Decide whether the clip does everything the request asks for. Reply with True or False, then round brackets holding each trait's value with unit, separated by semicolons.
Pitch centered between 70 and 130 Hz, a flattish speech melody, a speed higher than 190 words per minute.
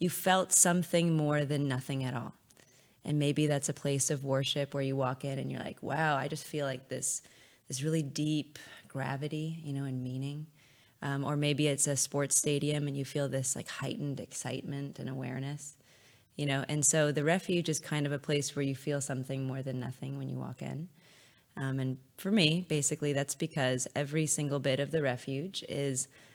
False (140 Hz; 2.0 semitones; 200 wpm)